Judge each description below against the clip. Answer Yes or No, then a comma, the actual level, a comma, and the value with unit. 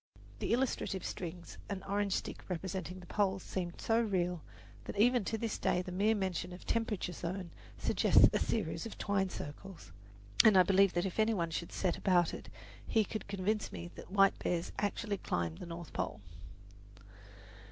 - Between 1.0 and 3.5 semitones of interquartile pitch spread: Yes, average, 2.7 semitones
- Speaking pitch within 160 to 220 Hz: Yes, high, 190 Hz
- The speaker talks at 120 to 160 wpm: No, average, 180 wpm